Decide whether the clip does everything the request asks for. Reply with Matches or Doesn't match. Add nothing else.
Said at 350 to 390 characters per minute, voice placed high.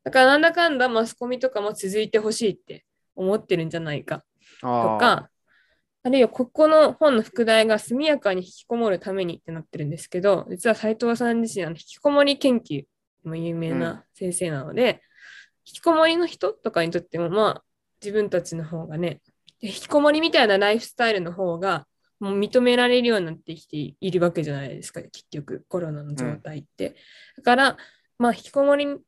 Matches